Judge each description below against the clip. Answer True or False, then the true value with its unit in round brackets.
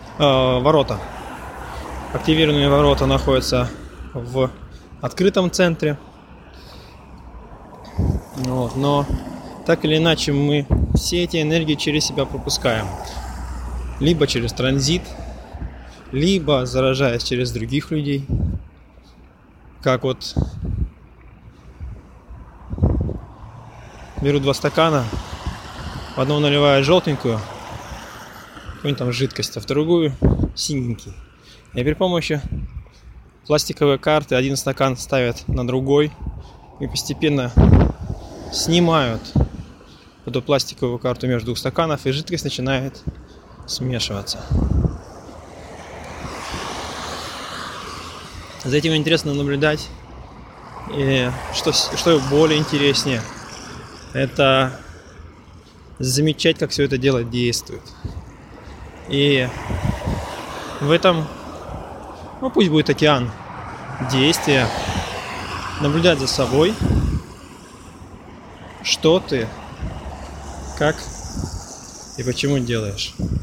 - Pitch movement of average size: False (6.5 semitones)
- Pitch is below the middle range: True (130 Hz)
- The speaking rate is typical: False (80 wpm)